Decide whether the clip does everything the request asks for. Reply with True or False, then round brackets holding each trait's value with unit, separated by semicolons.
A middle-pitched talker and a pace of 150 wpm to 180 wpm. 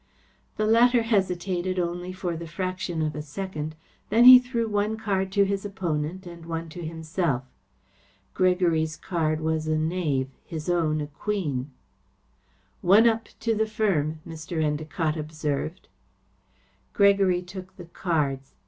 False (175 Hz; 140 wpm)